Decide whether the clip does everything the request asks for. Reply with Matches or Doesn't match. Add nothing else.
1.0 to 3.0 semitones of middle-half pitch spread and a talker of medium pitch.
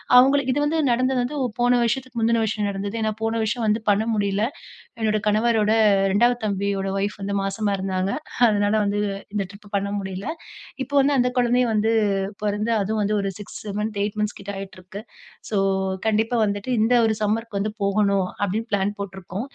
Doesn't match